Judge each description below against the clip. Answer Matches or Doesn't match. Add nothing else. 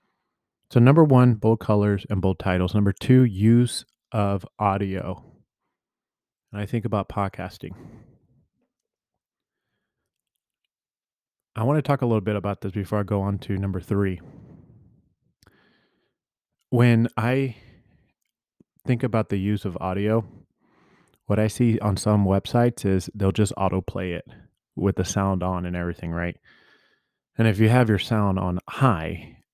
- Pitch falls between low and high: Doesn't match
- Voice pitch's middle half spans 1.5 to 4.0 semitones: Matches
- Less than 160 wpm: Matches